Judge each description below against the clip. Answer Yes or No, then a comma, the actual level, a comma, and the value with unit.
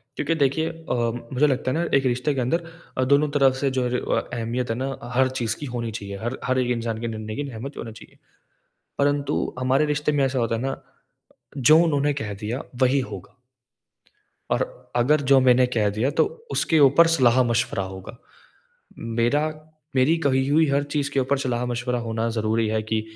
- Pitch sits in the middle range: No, low, 130 Hz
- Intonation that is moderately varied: Yes, average, 3.3 semitones